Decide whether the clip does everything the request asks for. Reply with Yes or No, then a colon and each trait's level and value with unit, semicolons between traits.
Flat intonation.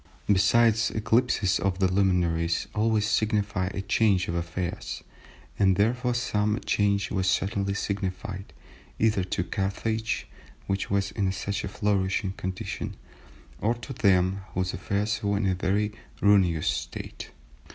Yes: narrow, 2.2 semitones